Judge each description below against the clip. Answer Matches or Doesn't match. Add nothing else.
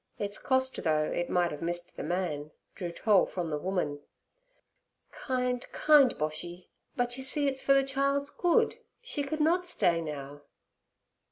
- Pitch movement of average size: Doesn't match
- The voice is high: Matches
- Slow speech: Doesn't match